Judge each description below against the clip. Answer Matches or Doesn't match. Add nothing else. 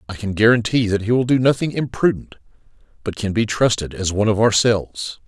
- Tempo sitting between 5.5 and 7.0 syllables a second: Matches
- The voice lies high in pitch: Doesn't match